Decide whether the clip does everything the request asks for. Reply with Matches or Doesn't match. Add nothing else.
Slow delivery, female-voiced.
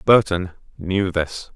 Doesn't match